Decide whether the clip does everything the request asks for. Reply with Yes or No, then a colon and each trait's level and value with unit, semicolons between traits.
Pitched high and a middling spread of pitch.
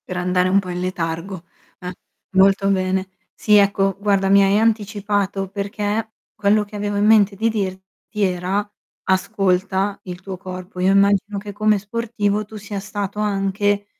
No: high, 200 Hz; narrow, 1.6 semitones